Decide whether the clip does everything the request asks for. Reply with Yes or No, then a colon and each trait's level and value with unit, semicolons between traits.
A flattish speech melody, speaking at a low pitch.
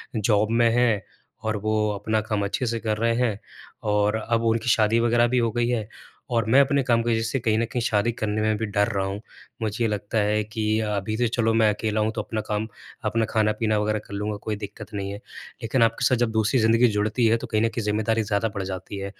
Yes: narrow, 1.6 semitones; low, 110 Hz